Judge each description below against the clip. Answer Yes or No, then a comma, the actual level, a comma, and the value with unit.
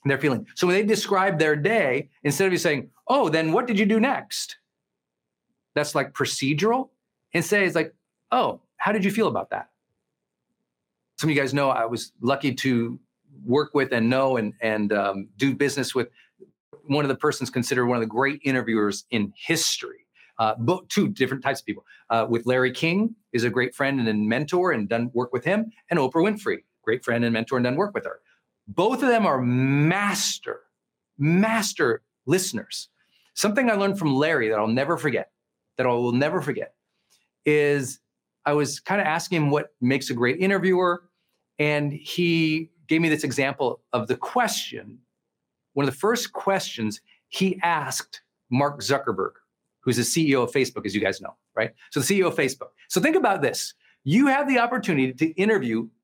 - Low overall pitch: No, medium, 150 Hz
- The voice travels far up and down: Yes, wide, 7.2 semitones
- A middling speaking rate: Yes, average, 185 wpm